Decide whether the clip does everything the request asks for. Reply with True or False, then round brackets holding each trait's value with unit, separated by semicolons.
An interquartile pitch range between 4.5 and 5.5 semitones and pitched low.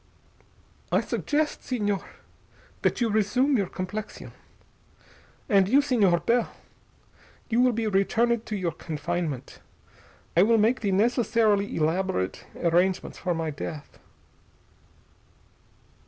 False (4.9 semitones; 205 Hz)